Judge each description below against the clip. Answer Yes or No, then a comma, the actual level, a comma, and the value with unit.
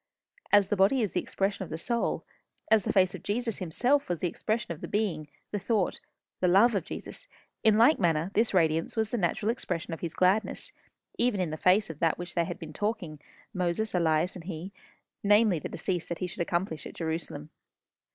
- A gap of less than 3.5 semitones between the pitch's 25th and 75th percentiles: No, average, 4.2 semitones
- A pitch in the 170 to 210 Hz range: Yes, medium, 185 Hz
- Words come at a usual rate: No, fast, 210 wpm